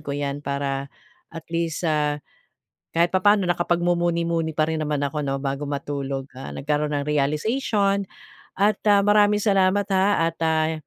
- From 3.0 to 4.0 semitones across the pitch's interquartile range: No, average, 4.5 semitones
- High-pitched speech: No, medium, 160 Hz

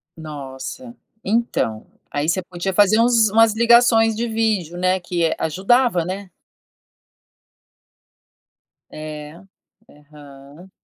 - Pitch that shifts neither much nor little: No, wide, 6.6 semitones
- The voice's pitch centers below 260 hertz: Yes, medium, 185 Hz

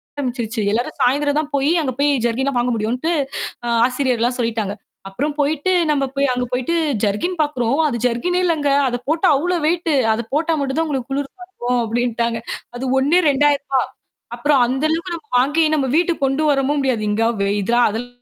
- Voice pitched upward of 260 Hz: Yes, very high, 270 Hz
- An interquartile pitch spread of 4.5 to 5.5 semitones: No, average, 3.8 semitones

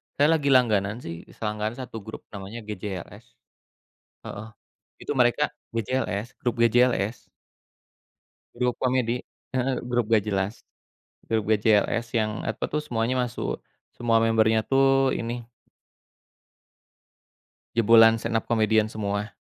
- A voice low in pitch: Yes, low, 115 Hz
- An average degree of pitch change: No, narrow, 2.3 semitones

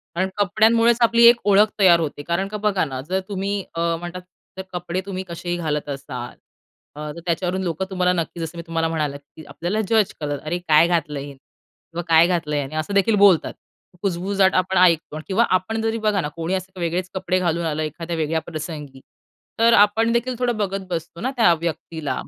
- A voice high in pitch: No, medium, 175 Hz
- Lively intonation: No, average, 3.5 semitones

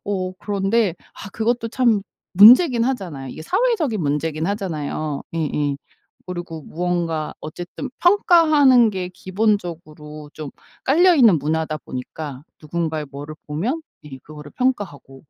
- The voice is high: No, medium, 180 Hz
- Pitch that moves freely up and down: Yes, wide, 7.1 semitones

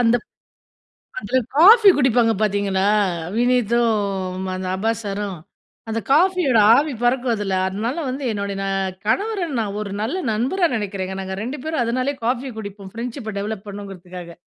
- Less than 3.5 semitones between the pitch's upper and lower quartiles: No, average, 4.5 semitones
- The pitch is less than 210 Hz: No, high, 225 Hz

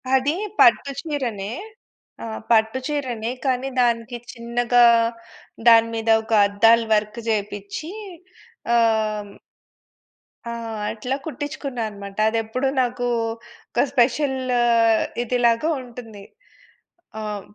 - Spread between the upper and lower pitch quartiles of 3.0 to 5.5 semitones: No, narrow, 2.6 semitones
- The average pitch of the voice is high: Yes, high, 235 Hz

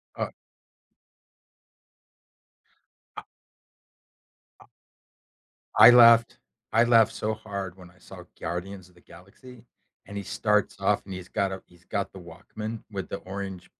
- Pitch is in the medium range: No, low, 100 Hz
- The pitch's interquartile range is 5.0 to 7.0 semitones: No, average, 3.0 semitones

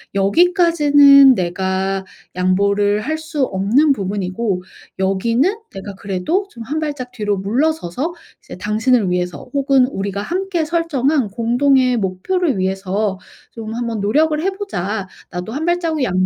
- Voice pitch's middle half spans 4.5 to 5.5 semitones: No, wide, 7.7 semitones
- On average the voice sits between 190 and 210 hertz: No, high, 230 Hz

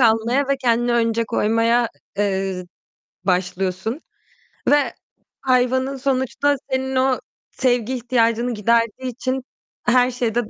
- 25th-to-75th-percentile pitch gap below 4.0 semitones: Yes, narrow, 2.4 semitones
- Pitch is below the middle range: No, high, 240 Hz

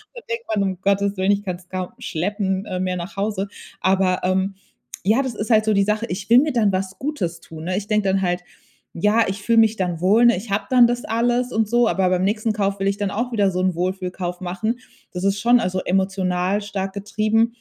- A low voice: No, high, 200 Hz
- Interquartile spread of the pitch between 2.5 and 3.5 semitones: Yes, average, 2.9 semitones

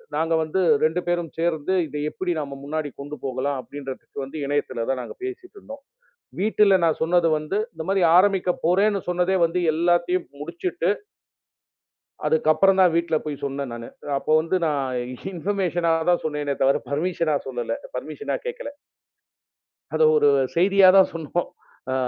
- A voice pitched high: No, medium, 165 Hz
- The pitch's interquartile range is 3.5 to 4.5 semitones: Yes, average, 4.0 semitones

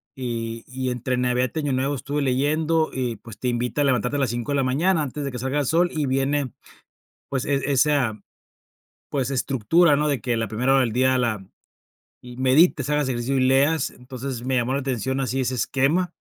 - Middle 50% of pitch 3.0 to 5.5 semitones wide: No, narrow, 2.6 semitones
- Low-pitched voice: Yes, low, 130 Hz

